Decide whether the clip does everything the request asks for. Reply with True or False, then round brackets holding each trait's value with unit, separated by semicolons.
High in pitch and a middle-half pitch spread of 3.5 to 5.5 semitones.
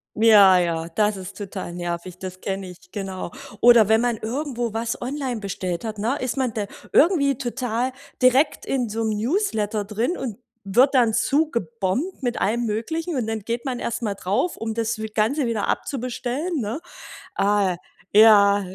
True (225 Hz; 3.9 semitones)